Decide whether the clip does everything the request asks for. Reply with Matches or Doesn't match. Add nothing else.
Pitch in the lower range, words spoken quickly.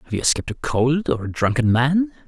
Matches